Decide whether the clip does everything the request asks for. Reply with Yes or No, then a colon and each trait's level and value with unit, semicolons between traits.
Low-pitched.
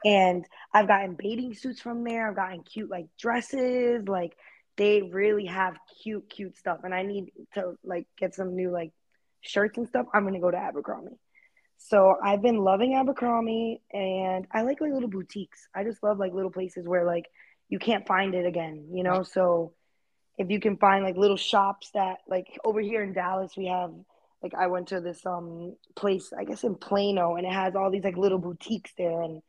No: high, 195 Hz